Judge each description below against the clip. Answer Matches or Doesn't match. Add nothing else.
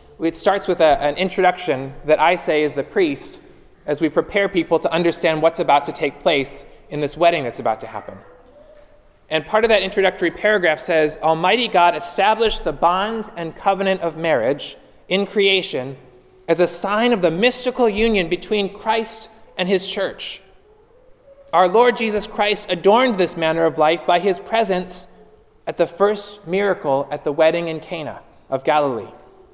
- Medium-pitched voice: Matches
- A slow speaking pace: Doesn't match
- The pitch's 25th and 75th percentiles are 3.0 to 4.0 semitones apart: Doesn't match